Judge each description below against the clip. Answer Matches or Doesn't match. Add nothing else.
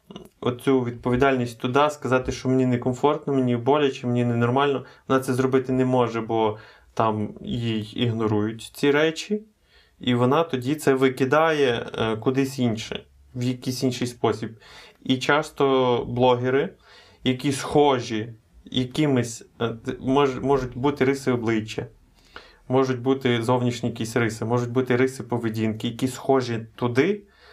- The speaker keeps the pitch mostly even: Matches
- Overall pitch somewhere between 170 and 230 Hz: Doesn't match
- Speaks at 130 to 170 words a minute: Doesn't match